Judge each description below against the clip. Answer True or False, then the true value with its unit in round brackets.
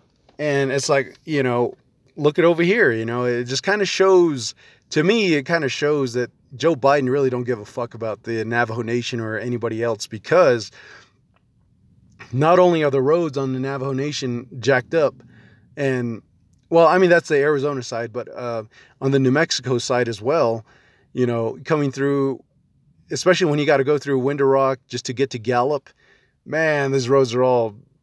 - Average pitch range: True (3.4 semitones)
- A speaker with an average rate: True (190 wpm)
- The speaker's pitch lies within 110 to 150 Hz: True (135 Hz)